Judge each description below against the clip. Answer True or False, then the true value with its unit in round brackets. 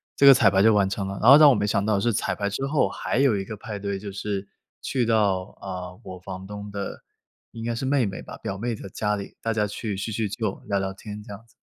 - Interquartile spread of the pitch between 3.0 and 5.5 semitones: False (2.5 semitones)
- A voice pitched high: False (105 Hz)